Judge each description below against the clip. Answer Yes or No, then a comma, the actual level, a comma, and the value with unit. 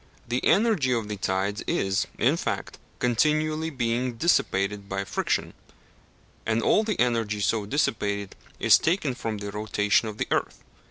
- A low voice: Yes, low, 115 Hz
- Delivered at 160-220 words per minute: No, average, 150 wpm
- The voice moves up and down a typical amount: Yes, average, 4.8 semitones